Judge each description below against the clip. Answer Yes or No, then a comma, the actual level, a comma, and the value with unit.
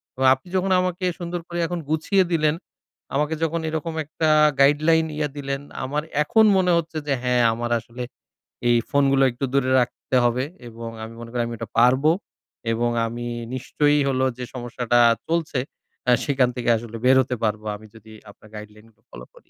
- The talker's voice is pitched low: Yes, low, 130 Hz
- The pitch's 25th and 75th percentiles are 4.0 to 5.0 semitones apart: Yes, average, 4.7 semitones